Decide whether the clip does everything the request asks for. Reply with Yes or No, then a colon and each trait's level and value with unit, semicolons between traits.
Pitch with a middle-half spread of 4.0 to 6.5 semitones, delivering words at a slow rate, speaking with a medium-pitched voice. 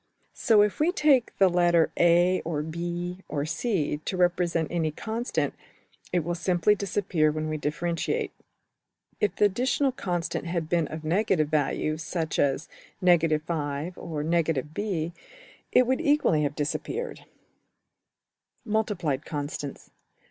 Yes: average, 4.3 semitones; slow, 120 wpm; medium, 170 Hz